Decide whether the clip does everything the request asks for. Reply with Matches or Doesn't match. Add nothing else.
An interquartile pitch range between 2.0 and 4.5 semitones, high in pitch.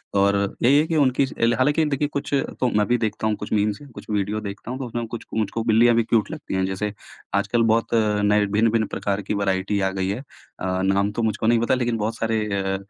Doesn't match